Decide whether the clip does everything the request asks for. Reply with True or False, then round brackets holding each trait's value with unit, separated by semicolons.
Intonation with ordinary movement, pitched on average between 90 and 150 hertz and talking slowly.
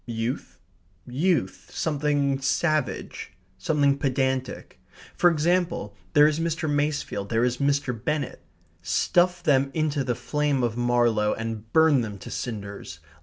True (4.1 semitones; 140 Hz; 125 wpm)